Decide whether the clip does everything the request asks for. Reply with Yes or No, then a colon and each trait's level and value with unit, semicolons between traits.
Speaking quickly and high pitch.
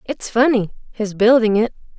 No: slow, 120 wpm; high, 225 Hz